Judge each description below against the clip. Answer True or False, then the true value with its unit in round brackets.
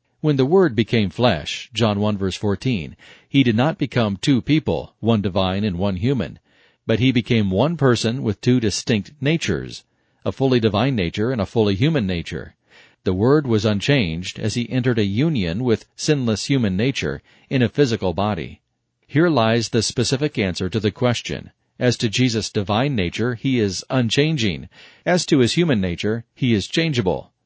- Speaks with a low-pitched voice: True (115 Hz)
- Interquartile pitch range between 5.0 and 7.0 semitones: False (4.3 semitones)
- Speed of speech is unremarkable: True (175 wpm)